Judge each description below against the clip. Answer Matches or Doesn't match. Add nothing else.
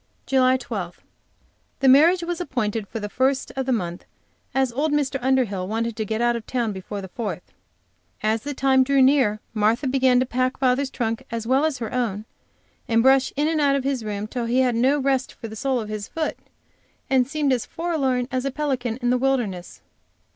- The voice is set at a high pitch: Matches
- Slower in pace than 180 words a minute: Doesn't match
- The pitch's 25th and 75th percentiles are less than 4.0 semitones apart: Matches